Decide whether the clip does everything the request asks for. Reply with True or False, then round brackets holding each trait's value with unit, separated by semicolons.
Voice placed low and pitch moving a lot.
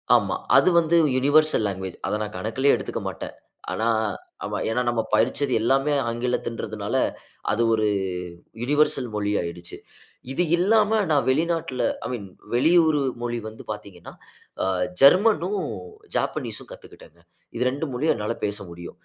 True (125 Hz; 6.2 semitones)